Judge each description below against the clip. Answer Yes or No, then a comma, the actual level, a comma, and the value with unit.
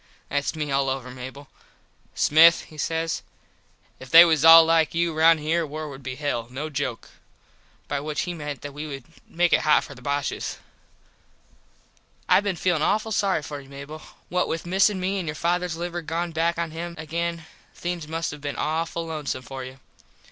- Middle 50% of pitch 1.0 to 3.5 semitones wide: Yes, average, 2.9 semitones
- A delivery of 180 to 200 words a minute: Yes, average, 190 wpm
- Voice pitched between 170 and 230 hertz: No, medium, 160 Hz